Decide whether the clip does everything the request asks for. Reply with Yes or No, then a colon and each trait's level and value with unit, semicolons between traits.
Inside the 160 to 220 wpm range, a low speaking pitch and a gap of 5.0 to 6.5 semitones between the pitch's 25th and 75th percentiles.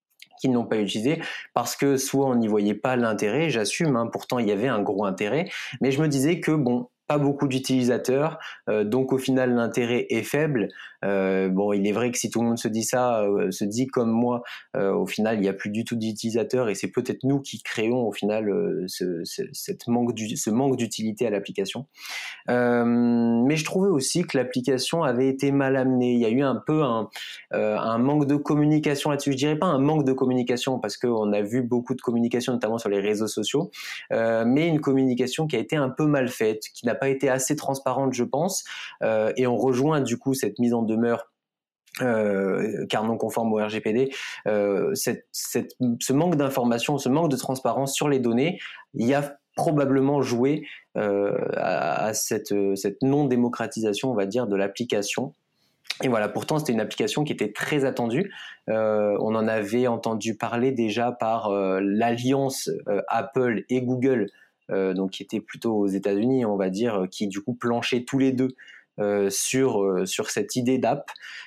No: average, 200 wpm; low, 125 Hz; average, 3.6 semitones